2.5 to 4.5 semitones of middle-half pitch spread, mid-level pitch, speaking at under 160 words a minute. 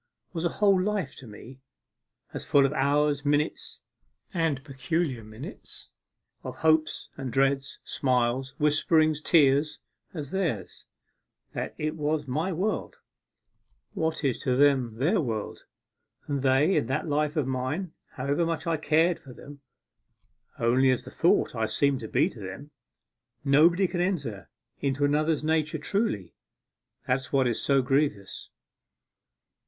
Yes: average, 3.3 semitones; medium, 145 Hz; average, 140 wpm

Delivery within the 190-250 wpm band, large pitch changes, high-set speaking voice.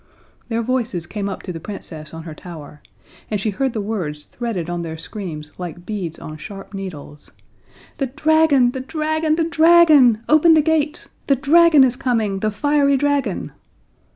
No: average, 170 wpm; wide, 8.7 semitones; high, 225 Hz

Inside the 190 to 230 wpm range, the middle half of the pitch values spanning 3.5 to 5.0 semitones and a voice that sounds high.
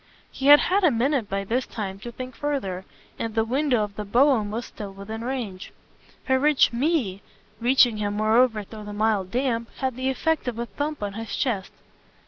Yes: average, 195 wpm; average, 4.1 semitones; high, 230 Hz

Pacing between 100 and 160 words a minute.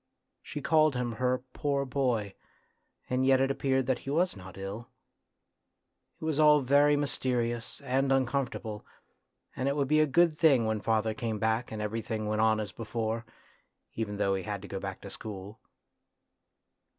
No: average, 170 wpm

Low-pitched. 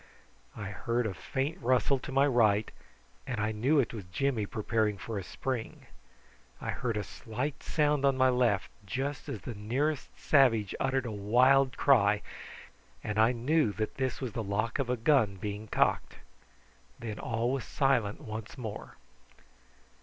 Yes: low, 120 Hz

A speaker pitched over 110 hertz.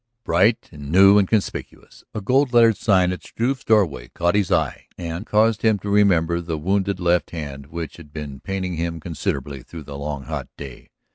No: very low, 85 Hz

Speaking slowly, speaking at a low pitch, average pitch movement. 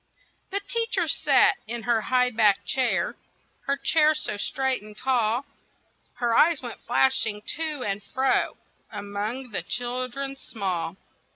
No: slow, 130 wpm; very high, 250 Hz; average, 4.0 semitones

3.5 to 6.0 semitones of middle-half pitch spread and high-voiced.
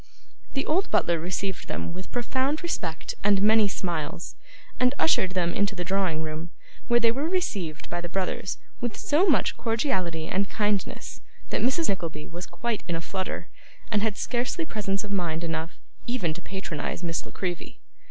Yes: wide, 5.6 semitones; high, 195 Hz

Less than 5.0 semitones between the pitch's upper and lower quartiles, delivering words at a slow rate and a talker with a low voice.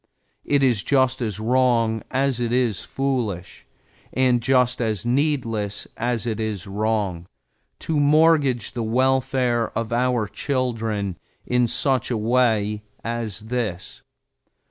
Yes: average, 3.0 semitones; slow, 120 wpm; low, 120 Hz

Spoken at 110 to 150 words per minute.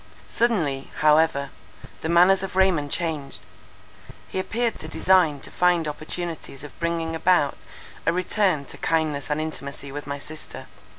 Yes: average, 140 wpm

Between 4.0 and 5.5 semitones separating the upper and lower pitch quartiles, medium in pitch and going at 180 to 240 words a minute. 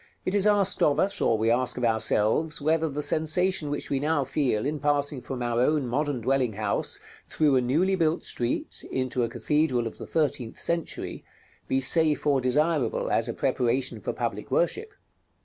Yes: average, 4.3 semitones; medium, 145 Hz; average, 185 wpm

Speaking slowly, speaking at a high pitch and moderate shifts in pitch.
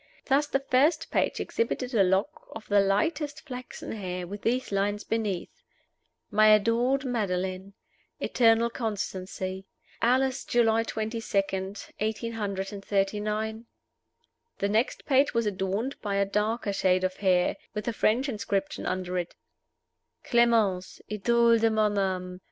Yes: slow, 125 wpm; high, 215 Hz; average, 3.3 semitones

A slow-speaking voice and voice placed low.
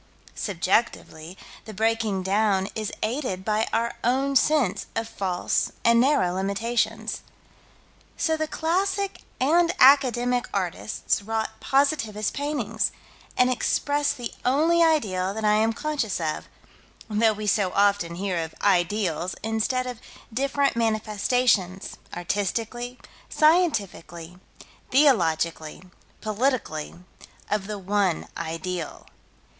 No: slow, 105 wpm; high, 220 Hz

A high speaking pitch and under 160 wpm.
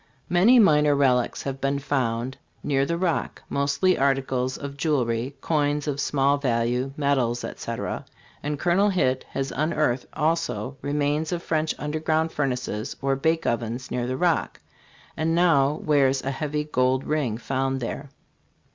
No: medium, 140 Hz; average, 145 wpm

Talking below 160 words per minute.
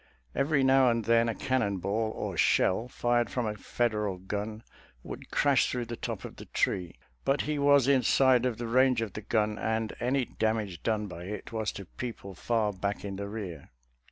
No: average, 195 wpm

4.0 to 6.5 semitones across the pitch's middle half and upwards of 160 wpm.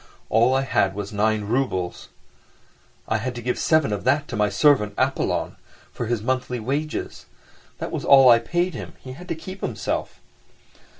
Yes: average, 4.5 semitones; average, 170 wpm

